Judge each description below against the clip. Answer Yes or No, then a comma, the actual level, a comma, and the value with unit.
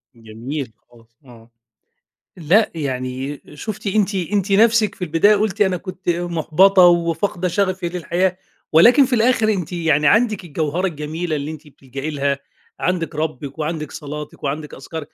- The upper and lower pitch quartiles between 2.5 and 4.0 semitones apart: No, average, 4.5 semitones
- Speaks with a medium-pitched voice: Yes, medium, 165 Hz